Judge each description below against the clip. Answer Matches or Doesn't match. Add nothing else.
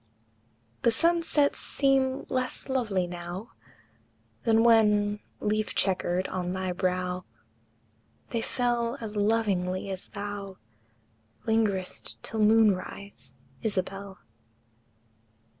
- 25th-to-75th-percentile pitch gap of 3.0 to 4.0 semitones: Matches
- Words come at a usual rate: Doesn't match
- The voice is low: Doesn't match